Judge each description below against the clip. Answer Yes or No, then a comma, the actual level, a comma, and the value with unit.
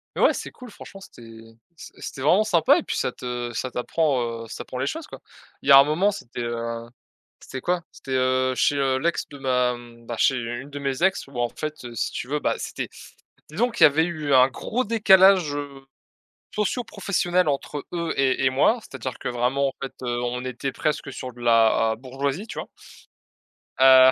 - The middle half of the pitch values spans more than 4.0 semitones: Yes, average, 5.1 semitones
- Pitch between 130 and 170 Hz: Yes, low, 135 Hz